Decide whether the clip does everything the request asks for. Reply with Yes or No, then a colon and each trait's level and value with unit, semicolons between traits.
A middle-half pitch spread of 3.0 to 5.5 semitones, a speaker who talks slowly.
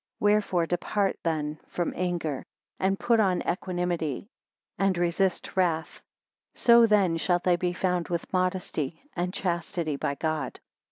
No: narrow, 2.4 semitones; slow, 130 wpm